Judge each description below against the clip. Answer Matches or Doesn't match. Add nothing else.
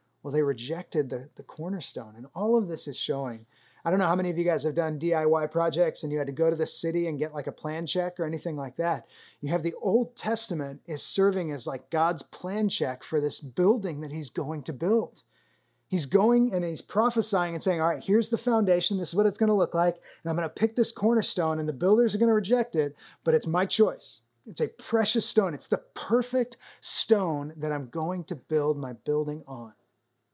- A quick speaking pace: Matches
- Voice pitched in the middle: Matches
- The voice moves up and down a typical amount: Matches